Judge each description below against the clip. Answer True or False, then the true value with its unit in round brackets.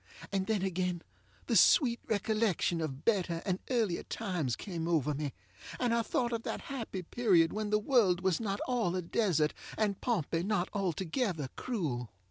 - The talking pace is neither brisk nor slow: True (165 wpm)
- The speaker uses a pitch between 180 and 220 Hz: True (190 Hz)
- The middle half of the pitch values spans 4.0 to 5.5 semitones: True (4.9 semitones)